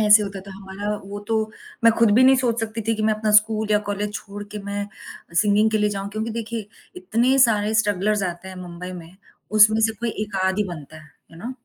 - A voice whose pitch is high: Yes, high, 210 Hz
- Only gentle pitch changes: Yes, narrow, 1.9 semitones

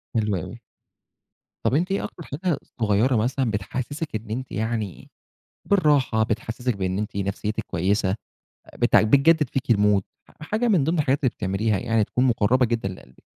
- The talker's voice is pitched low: Yes, low, 115 Hz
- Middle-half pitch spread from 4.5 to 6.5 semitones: Yes, average, 4.9 semitones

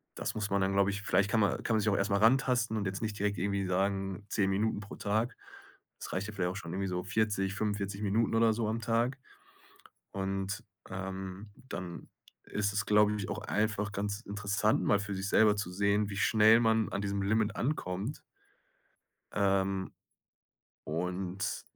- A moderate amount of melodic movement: No, narrow, 1.8 semitones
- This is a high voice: No, low, 100 Hz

